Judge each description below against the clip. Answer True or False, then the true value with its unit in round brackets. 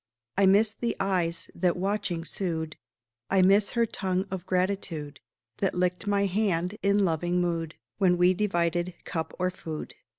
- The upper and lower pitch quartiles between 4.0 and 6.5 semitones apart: False (2.5 semitones)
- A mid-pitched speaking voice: True (180 Hz)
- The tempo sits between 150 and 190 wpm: True (155 wpm)